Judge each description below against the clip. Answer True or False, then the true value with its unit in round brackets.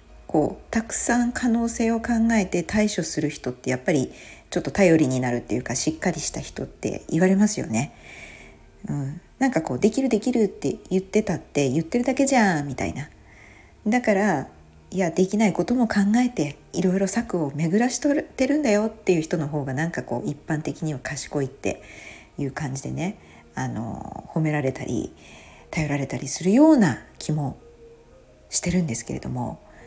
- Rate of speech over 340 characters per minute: True (350 characters per minute)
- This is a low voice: False (165 Hz)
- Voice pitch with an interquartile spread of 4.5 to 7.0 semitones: False (8.0 semitones)